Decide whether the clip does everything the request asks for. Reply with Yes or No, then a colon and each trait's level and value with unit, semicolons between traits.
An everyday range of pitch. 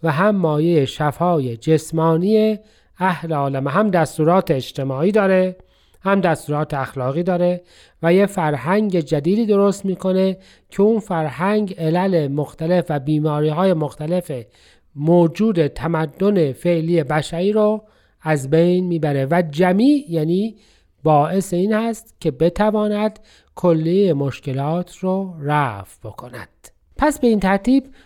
Yes: average, 4.1 semitones